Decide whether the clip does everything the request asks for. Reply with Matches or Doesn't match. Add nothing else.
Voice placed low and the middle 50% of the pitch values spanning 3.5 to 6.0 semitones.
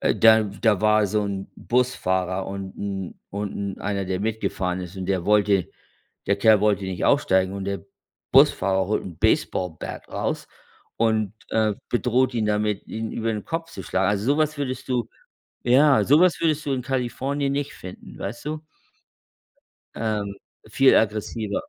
Matches